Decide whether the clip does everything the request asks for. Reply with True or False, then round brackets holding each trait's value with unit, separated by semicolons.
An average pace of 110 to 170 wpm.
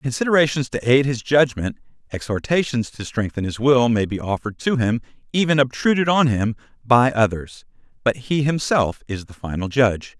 True (165 wpm)